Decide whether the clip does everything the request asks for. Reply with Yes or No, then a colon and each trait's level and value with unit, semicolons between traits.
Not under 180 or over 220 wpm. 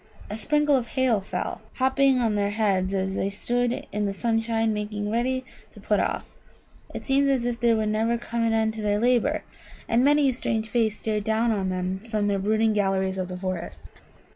Yes: fast, 205 wpm